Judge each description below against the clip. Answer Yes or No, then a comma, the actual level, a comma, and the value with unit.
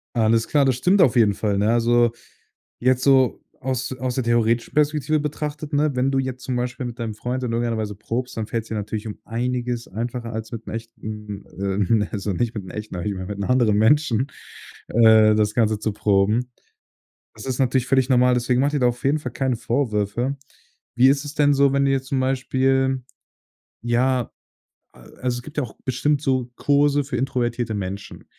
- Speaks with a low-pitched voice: Yes, low, 120 Hz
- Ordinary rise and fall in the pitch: Yes, average, 3.3 semitones